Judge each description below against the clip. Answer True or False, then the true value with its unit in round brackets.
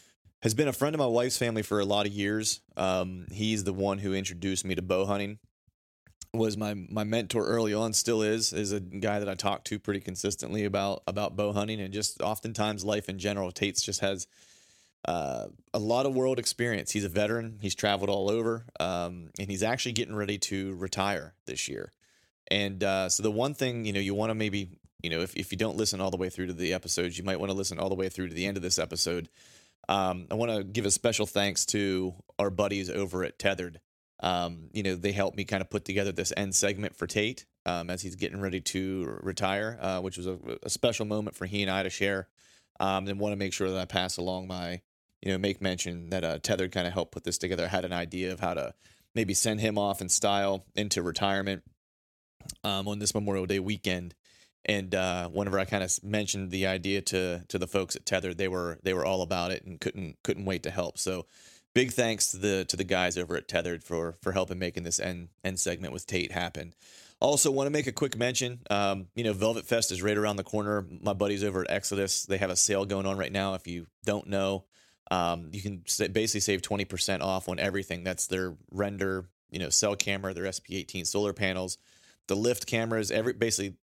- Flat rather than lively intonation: True (2.1 semitones)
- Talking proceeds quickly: True (230 wpm)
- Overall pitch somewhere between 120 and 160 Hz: False (100 Hz)